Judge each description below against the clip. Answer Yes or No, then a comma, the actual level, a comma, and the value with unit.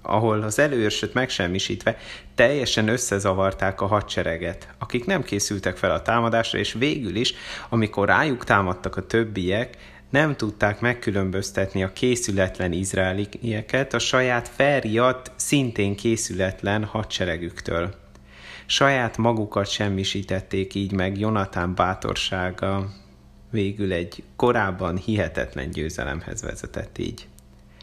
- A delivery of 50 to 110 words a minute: Yes, slow, 105 wpm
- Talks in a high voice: No, low, 100 Hz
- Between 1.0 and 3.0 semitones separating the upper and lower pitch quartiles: No, average, 3.7 semitones